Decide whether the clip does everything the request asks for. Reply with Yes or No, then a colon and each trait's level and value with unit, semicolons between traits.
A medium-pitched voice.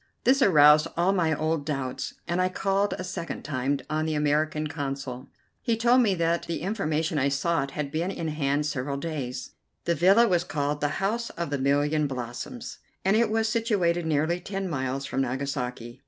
Yes: medium, 155 Hz